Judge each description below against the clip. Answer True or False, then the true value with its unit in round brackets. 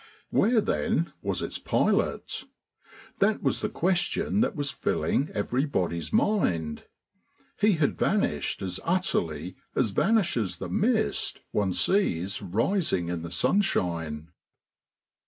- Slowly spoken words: True (115 wpm)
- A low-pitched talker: True (130 Hz)